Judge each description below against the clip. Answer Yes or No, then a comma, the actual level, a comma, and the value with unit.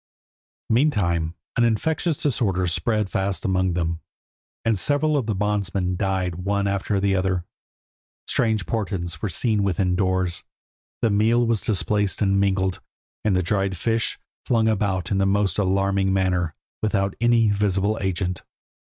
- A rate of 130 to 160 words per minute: Yes, average, 145 wpm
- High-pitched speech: No, low, 100 Hz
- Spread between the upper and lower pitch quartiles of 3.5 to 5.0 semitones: No, narrow, 2.6 semitones